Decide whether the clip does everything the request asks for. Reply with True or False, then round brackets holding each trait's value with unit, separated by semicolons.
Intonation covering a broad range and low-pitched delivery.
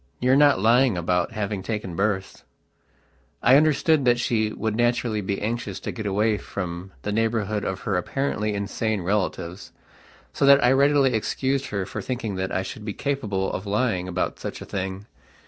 False (4.2 semitones; 105 Hz)